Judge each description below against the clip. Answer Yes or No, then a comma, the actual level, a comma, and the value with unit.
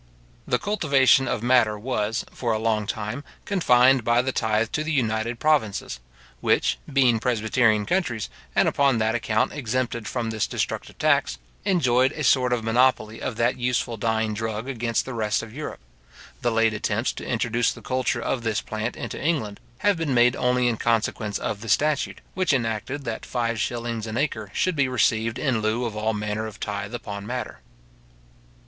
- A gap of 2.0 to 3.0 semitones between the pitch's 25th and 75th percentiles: Yes, average, 2.7 semitones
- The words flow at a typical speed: Yes, average, 180 wpm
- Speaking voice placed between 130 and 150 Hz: No, low, 115 Hz